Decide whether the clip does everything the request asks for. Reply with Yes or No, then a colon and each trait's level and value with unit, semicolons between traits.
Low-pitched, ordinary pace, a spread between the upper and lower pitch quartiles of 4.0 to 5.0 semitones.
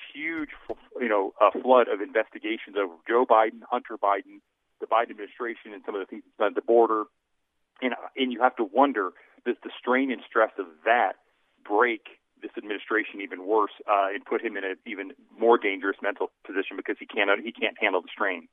Yes: low, 115 Hz; average, 195 wpm; average, 4.5 semitones